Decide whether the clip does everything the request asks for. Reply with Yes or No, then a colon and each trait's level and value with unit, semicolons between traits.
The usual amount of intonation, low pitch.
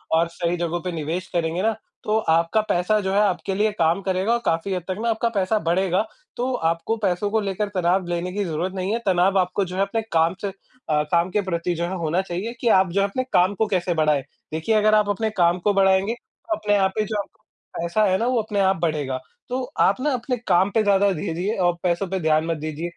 No: average, 3.4 semitones; high, 190 Hz